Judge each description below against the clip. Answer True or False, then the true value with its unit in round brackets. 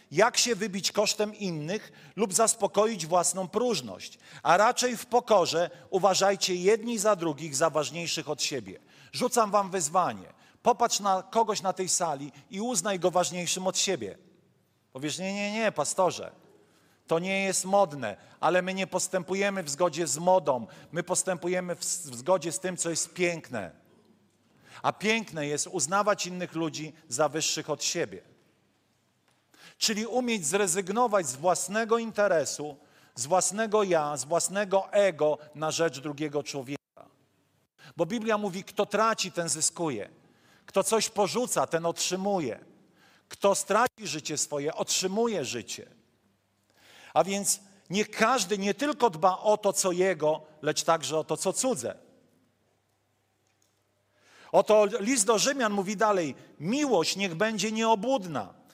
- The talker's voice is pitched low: False (185 Hz)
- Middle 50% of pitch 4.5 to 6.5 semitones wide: True (4.8 semitones)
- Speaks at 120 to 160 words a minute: True (135 wpm)